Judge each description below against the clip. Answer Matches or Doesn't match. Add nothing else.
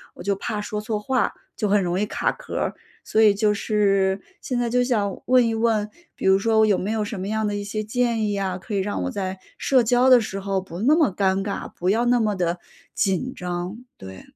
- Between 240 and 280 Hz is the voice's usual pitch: Doesn't match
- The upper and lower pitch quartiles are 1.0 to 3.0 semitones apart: Matches